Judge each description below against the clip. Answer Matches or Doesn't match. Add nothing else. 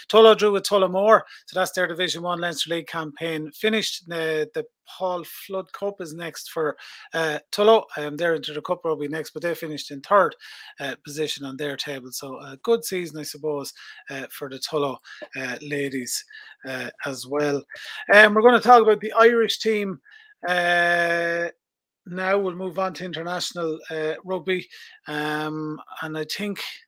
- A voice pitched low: Doesn't match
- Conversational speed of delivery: Matches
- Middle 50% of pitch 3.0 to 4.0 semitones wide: Doesn't match